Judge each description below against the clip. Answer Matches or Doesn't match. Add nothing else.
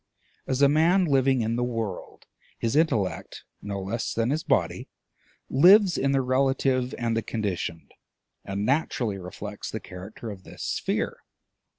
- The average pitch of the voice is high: Doesn't match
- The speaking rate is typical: Matches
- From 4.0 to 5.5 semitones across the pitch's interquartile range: Matches